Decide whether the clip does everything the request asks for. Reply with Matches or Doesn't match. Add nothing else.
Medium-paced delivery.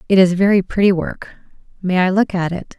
Matches